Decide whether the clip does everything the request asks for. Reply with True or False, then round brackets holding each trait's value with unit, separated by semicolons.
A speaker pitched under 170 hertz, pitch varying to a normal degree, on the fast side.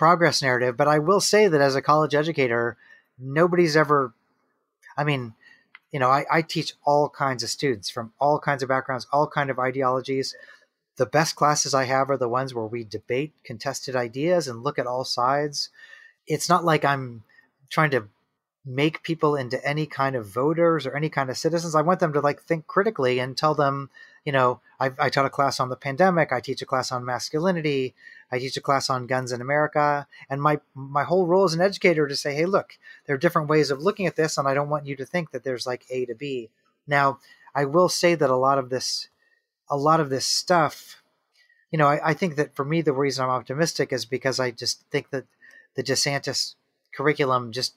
True (140 Hz; 3.3 semitones; 215 wpm)